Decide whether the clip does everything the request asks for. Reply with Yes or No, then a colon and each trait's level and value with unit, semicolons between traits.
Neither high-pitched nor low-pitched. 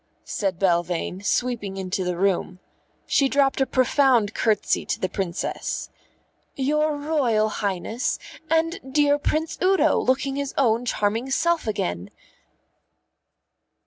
No: high, 240 Hz